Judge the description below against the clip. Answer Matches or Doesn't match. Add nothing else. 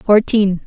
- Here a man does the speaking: Doesn't match